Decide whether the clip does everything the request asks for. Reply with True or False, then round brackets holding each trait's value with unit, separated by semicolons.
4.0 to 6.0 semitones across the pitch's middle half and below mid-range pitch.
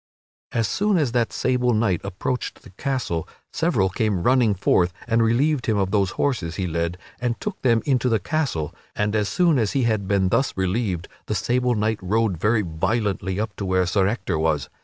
True (4.7 semitones; 110 Hz)